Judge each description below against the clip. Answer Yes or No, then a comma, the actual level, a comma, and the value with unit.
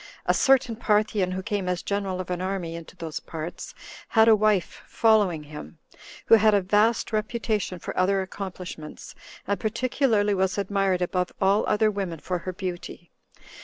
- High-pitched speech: Yes, high, 195 Hz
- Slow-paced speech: No, average, 165 wpm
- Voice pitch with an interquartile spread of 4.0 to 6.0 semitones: No, average, 2.9 semitones